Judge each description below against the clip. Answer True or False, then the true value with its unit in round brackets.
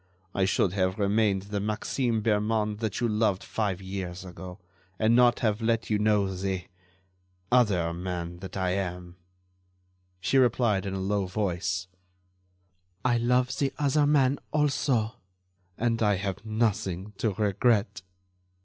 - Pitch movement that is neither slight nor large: True (3.5 semitones)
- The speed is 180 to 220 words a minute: False (140 wpm)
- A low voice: True (105 Hz)